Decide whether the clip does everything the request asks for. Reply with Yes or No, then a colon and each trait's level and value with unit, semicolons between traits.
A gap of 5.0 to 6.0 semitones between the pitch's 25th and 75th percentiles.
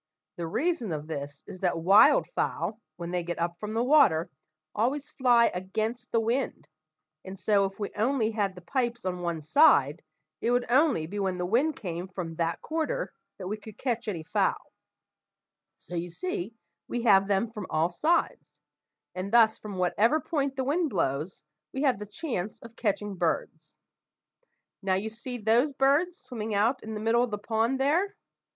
Yes: wide, 5.5 semitones